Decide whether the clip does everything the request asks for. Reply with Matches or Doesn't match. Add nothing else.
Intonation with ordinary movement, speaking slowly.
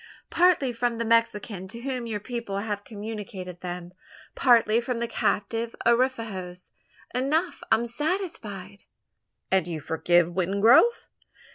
Matches